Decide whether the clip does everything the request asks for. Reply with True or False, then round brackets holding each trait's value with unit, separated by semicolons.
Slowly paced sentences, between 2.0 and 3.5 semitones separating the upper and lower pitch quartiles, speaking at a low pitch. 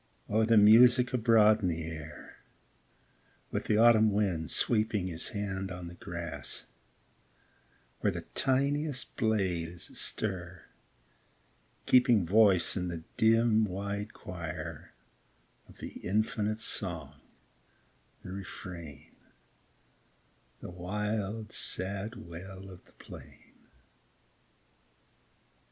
False (100 wpm; 3.9 semitones; 100 Hz)